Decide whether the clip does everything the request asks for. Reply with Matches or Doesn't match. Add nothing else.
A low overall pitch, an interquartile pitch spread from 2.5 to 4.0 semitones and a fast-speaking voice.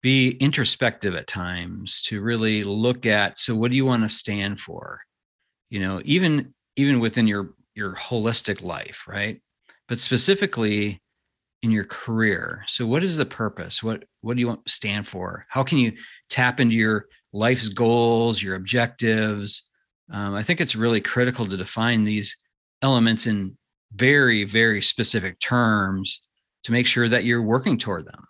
Doesn't match